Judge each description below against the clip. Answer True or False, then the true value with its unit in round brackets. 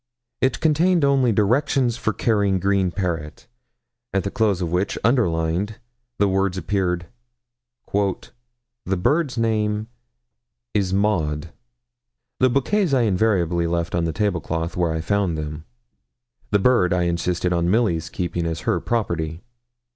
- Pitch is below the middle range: True (100 Hz)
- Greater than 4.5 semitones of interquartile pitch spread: True (5.0 semitones)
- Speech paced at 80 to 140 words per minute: True (135 wpm)